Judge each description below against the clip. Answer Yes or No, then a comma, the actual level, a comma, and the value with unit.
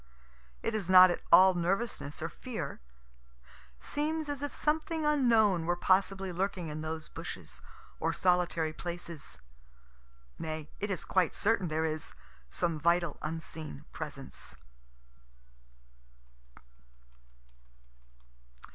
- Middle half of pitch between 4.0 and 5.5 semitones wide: Yes, average, 4.3 semitones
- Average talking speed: No, slow, 105 wpm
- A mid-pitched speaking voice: Yes, medium, 180 Hz